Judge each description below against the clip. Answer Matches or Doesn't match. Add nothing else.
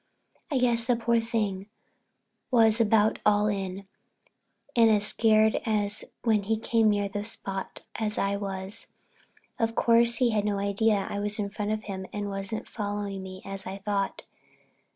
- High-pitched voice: Matches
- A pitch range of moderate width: Doesn't match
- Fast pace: Doesn't match